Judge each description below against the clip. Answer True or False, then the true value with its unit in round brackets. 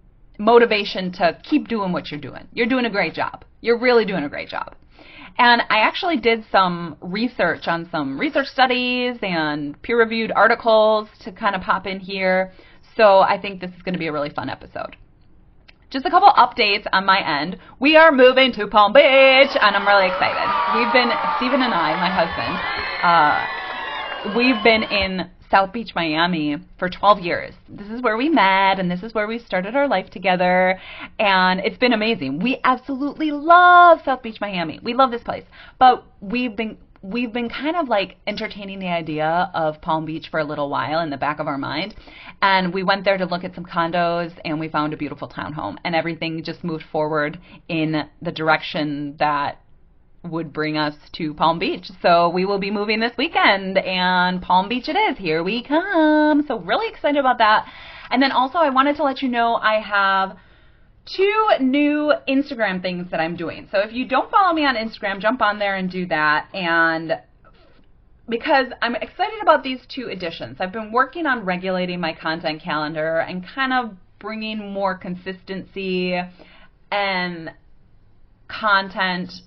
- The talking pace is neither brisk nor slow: True (185 wpm)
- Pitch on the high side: True (200 Hz)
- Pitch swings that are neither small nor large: False (6.3 semitones)